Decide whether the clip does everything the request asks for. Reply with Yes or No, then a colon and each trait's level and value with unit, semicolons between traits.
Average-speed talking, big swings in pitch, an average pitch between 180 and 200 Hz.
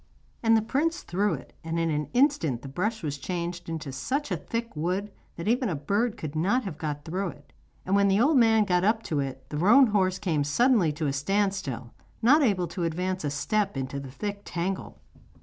No: fast, 220 wpm; wide, 6.3 semitones; medium, 185 Hz